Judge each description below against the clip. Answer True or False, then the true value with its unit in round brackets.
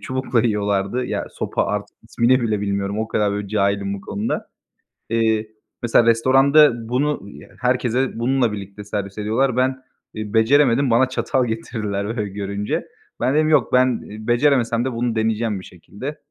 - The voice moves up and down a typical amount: True (3.7 semitones)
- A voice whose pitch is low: True (115 Hz)